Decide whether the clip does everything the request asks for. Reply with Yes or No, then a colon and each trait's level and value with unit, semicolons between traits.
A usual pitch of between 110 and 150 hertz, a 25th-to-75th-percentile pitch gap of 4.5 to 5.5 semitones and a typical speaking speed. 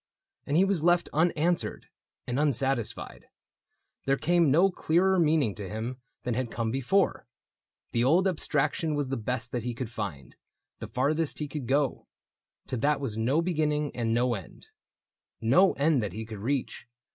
Yes: low, 135 Hz; average, 5.0 semitones; average, 170 wpm